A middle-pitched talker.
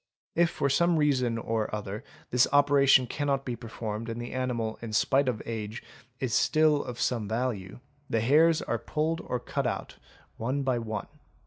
No: low, 125 Hz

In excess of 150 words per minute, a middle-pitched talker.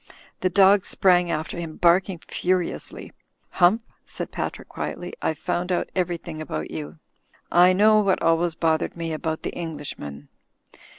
No: average, 140 wpm; medium, 175 Hz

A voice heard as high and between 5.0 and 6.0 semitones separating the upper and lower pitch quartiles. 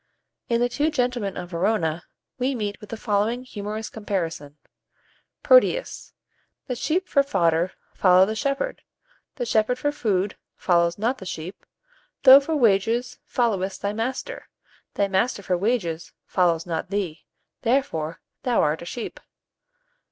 Yes: high, 210 Hz; wide, 5.5 semitones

